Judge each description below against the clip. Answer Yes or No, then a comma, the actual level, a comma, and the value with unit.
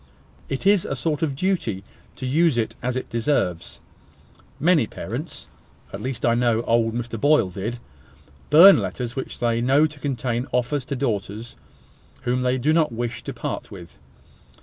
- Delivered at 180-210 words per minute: No, average, 165 wpm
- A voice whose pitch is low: Yes, low, 125 Hz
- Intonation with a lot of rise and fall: No, average, 3.9 semitones